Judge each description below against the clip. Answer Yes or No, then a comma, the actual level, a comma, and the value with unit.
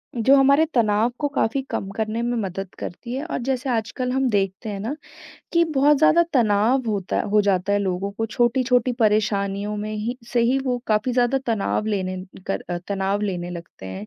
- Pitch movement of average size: Yes, average, 4.2 semitones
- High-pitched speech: Yes, high, 220 Hz